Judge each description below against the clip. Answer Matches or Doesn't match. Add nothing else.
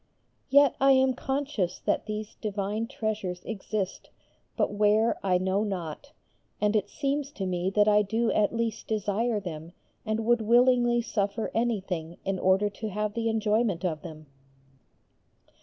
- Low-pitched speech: Doesn't match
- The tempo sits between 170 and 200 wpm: Doesn't match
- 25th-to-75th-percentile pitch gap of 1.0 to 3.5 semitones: Matches